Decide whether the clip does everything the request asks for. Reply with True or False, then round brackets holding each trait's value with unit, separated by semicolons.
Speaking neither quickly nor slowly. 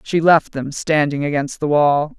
True (190 wpm)